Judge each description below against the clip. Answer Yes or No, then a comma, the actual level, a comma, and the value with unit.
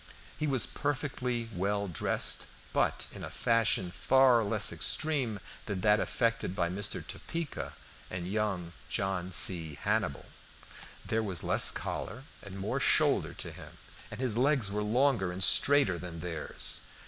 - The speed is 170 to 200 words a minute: No, average, 145 wpm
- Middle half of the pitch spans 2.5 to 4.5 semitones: No, average, 5.3 semitones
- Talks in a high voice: No, low, 105 Hz